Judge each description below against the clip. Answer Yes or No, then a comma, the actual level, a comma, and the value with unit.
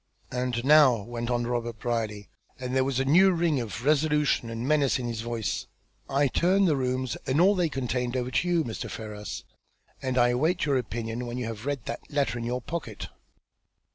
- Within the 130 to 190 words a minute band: No, average, 200 wpm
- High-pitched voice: No, low, 125 Hz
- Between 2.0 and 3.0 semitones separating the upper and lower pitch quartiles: No, average, 3.6 semitones